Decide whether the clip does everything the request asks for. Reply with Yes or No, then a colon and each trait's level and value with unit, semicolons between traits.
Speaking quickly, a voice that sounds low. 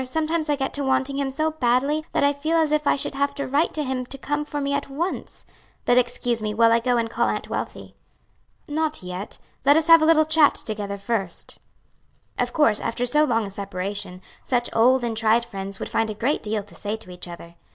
No: fast, 230 wpm; very high, 255 Hz